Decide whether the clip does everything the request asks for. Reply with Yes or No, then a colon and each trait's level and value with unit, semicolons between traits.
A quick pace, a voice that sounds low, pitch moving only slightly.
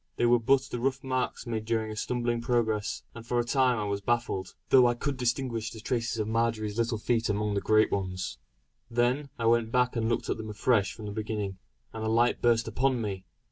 Yes: fast, 220 wpm; low, 115 Hz; narrow, 2.1 semitones